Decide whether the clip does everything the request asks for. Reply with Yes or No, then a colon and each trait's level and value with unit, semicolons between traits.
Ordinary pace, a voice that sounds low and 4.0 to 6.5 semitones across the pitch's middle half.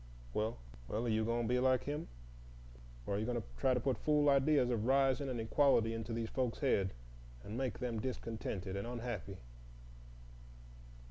No: average, 175 wpm; low, 120 Hz; average, 3.2 semitones